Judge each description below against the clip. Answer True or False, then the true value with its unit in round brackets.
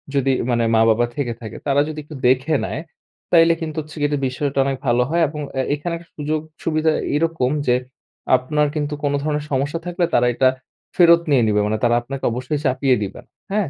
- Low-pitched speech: False (145 Hz)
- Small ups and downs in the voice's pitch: False (3.5 semitones)